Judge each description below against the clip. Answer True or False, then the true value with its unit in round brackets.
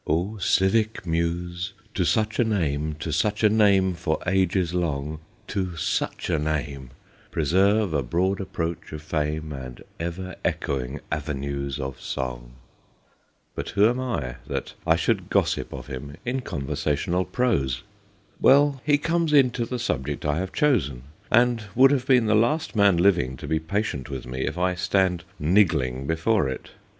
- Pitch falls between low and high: False (85 Hz)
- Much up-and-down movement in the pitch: True (6.5 semitones)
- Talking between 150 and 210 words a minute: True (160 wpm)